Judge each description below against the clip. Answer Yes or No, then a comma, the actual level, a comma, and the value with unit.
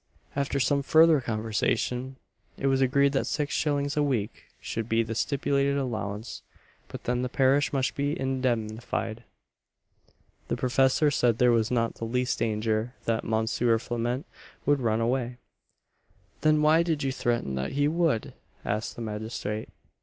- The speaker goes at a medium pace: Yes, average, 150 wpm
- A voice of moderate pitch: No, low, 125 Hz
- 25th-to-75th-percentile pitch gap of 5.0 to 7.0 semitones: No, average, 3.7 semitones